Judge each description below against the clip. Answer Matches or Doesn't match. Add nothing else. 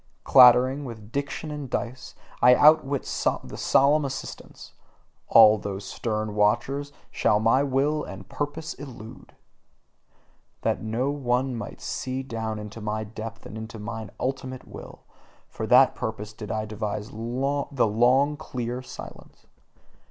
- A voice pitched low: Matches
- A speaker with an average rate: Doesn't match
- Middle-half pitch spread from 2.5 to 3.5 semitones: Doesn't match